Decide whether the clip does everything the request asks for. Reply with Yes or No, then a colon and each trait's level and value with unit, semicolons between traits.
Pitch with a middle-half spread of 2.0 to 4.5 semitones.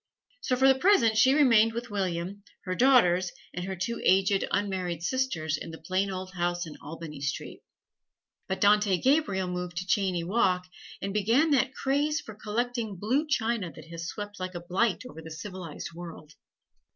No: average, 5.0 semitones